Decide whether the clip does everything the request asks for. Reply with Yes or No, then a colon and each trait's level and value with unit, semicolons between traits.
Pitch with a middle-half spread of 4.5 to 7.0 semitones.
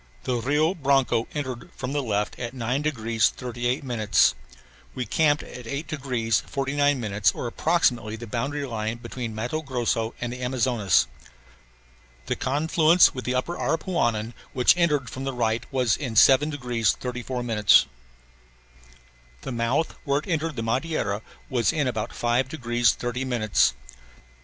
No: average, 3.4 semitones